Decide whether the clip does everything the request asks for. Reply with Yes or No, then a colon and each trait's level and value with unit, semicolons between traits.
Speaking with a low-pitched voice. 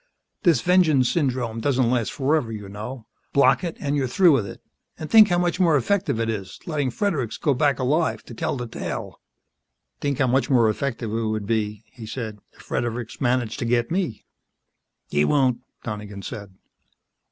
Yes: low, 125 Hz